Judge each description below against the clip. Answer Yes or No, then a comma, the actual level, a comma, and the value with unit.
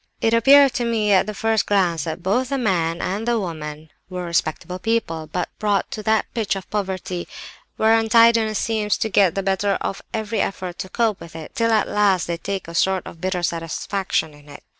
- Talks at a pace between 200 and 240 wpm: Yes, fast, 205 wpm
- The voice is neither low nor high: No, high, 195 Hz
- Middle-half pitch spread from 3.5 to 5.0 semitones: Yes, average, 4.3 semitones